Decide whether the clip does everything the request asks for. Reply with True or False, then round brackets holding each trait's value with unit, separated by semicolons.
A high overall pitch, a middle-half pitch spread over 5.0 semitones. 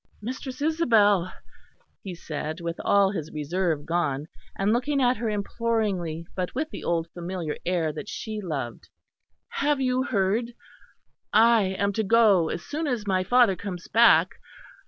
True (200 Hz; 5.4 semitones)